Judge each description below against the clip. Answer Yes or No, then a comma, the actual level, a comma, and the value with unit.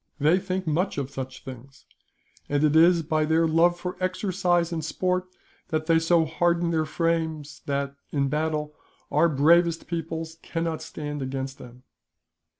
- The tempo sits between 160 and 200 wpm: No, average, 150 wpm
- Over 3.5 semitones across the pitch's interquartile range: No, narrow, 2.6 semitones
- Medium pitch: Yes, medium, 160 Hz